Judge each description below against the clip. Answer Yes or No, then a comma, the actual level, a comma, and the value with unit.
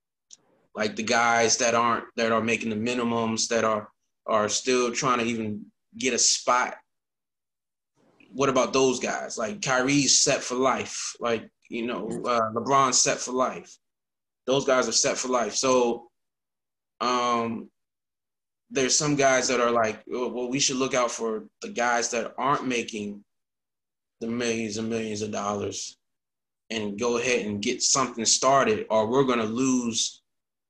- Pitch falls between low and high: No, low, 115 Hz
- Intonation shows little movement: Yes, narrow, 2.3 semitones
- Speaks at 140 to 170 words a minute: Yes, average, 155 wpm